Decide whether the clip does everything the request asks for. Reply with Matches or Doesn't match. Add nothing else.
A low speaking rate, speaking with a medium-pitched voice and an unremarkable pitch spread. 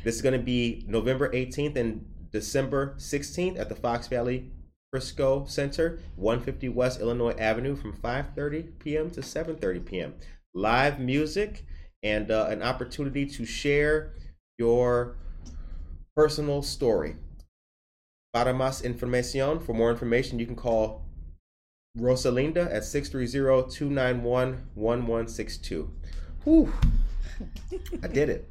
Doesn't match